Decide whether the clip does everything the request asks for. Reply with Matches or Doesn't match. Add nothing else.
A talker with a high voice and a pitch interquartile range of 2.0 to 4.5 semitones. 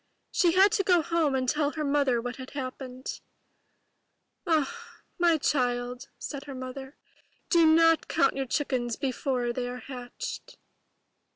Matches